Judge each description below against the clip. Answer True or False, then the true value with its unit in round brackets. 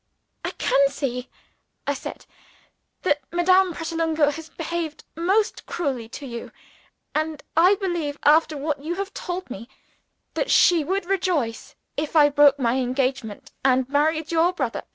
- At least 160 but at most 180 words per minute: False (145 wpm)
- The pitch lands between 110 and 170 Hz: False (310 Hz)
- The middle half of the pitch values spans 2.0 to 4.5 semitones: True (3.9 semitones)